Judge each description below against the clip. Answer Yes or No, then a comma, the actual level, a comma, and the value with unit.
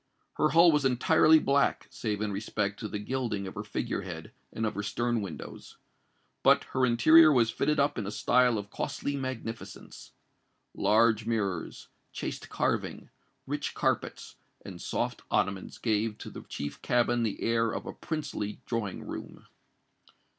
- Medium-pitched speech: No, low, 115 Hz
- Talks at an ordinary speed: Yes, average, 155 wpm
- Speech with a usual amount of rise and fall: Yes, average, 3.9 semitones